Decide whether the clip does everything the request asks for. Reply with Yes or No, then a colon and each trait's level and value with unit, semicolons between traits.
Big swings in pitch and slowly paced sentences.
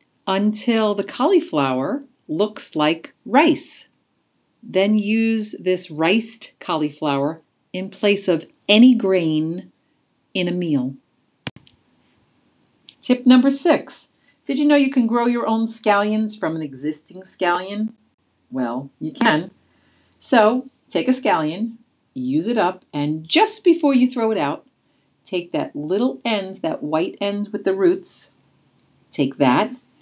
Yes: wide, 6.6 semitones; slow, 130 wpm